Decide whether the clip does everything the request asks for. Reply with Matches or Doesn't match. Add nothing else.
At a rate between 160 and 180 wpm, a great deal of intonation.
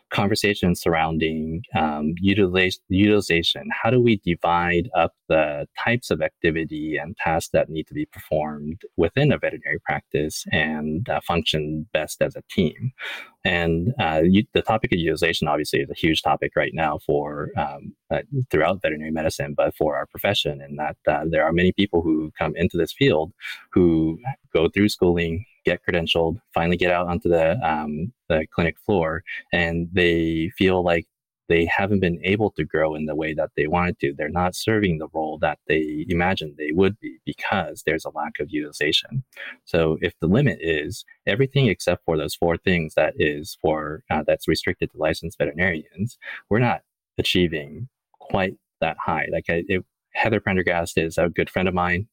Doesn't match